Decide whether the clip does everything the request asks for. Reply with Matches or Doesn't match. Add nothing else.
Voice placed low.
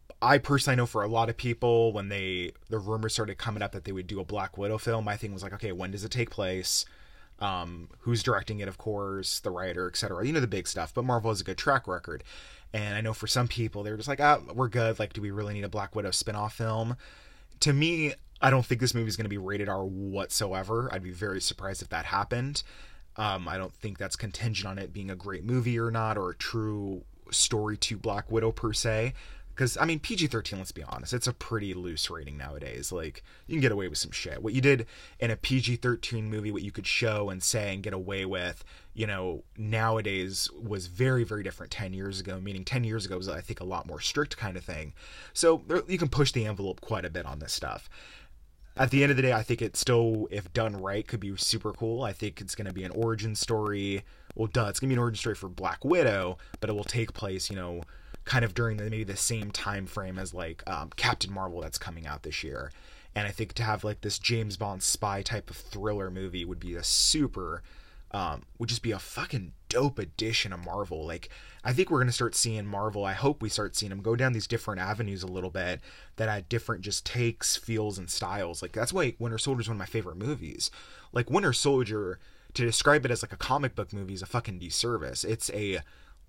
Matches